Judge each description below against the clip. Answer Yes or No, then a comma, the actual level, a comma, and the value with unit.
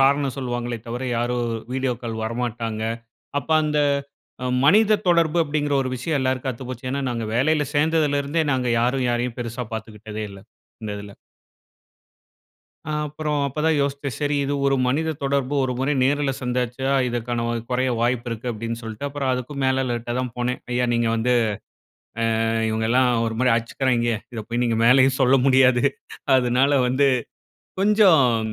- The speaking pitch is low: Yes, low, 125 Hz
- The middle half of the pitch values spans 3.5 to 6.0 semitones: No, average, 2.9 semitones